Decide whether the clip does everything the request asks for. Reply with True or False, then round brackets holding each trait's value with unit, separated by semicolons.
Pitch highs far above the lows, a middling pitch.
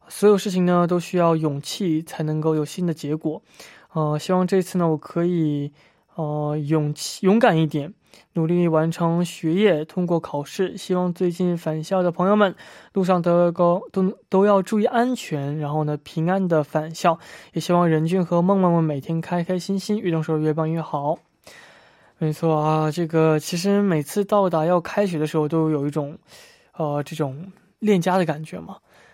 False (3.1 semitones; 170 Hz)